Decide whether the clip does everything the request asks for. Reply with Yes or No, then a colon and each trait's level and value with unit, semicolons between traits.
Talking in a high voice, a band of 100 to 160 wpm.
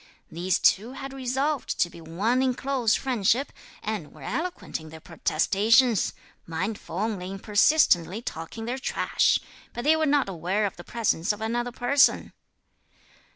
Yes: high, 225 Hz; average, 155 wpm